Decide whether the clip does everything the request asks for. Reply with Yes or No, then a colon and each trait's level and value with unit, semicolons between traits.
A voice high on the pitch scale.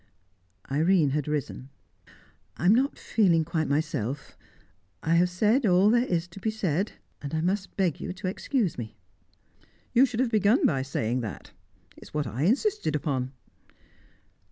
No: medium, 170 Hz